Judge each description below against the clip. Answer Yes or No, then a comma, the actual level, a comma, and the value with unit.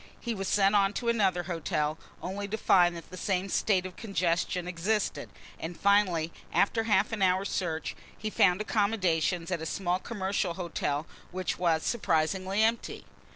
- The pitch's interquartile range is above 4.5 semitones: No, average, 2.7 semitones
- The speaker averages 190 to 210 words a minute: No, average, 160 wpm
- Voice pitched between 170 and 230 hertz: Yes, medium, 185 Hz